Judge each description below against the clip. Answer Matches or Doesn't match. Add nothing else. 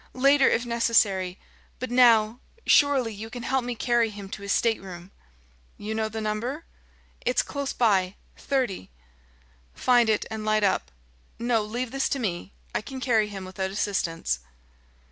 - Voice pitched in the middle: Doesn't match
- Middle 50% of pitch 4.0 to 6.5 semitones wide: Doesn't match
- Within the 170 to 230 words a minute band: Doesn't match